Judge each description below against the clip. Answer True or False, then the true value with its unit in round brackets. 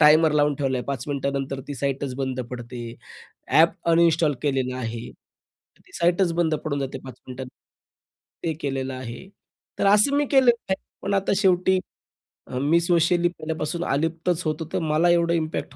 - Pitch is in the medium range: True (155 Hz)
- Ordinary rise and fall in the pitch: True (4.2 semitones)